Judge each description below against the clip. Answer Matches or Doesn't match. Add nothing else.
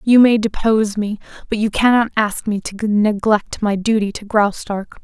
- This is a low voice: Doesn't match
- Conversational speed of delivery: Matches